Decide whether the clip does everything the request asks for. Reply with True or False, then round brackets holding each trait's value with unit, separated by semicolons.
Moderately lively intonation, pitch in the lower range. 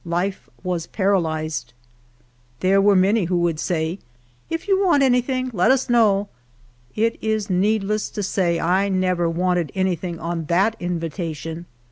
False (3.8 semitones; 185 Hz)